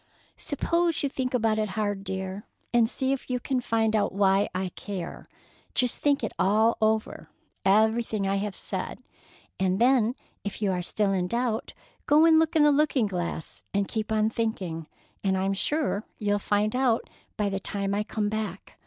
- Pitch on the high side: Yes, high, 215 Hz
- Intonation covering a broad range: No, average, 3.7 semitones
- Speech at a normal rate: Yes, average, 180 wpm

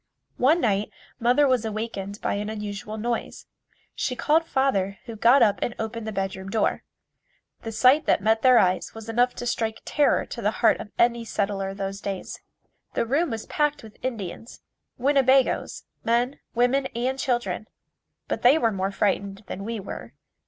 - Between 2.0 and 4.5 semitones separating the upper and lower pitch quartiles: Yes, average, 3.7 semitones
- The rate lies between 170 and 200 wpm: Yes, average, 175 wpm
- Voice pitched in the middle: No, high, 225 Hz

